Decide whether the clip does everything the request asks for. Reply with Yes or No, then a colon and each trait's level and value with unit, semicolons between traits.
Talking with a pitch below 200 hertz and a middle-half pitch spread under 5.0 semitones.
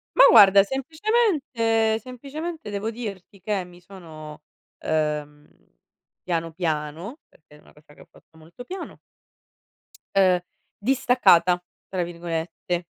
No: high, 190 Hz; wide, 6.7 semitones